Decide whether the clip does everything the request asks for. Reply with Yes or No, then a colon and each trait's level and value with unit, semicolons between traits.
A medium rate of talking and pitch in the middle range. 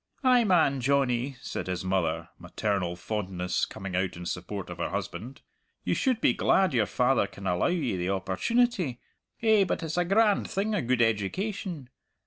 No: average, 170 wpm; low, 125 Hz